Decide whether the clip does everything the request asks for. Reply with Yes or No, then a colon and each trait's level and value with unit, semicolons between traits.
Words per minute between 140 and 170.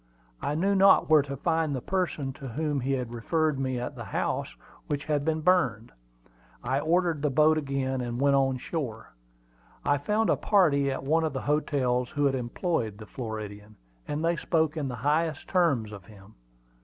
No: average, 190 wpm